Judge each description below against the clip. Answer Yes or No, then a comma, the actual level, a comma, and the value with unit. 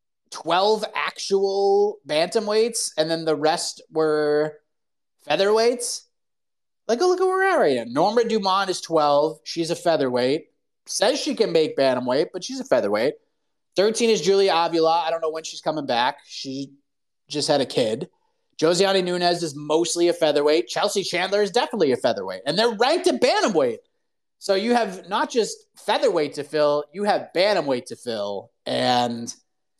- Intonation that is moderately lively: No, wide, 7.8 semitones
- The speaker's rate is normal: Yes, average, 165 wpm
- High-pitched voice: No, medium, 180 Hz